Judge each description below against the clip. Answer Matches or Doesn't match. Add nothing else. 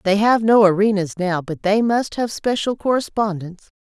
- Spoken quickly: Doesn't match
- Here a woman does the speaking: Matches